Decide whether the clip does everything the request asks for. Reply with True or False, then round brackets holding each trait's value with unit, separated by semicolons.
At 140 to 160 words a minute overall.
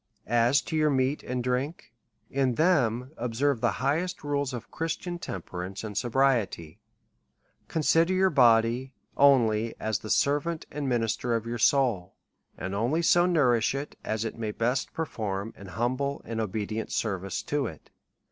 True (155 wpm)